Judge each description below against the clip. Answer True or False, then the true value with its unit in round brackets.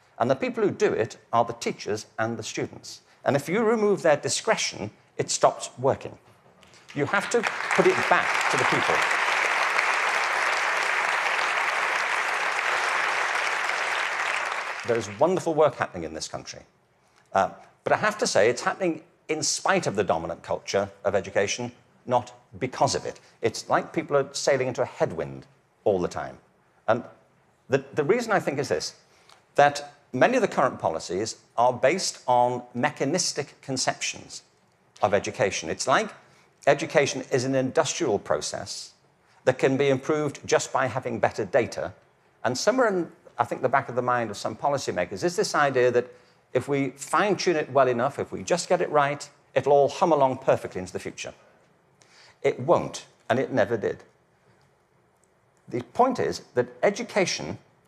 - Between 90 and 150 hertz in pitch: True (140 Hz)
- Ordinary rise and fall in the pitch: True (4.6 semitones)